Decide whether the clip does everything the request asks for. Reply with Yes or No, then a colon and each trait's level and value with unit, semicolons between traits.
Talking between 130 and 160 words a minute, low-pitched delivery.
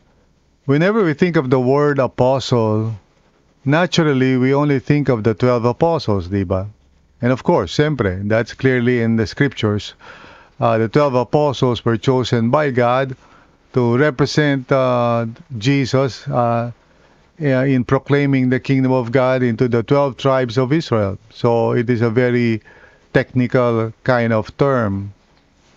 Yes: slow, 135 wpm; low, 125 Hz